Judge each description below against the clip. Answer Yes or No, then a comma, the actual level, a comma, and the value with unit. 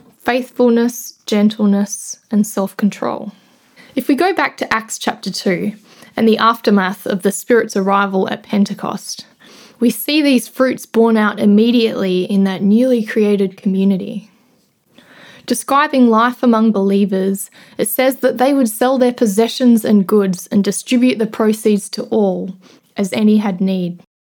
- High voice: Yes, high, 220 Hz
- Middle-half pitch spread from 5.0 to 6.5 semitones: No, average, 3.4 semitones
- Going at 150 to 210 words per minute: No, average, 140 wpm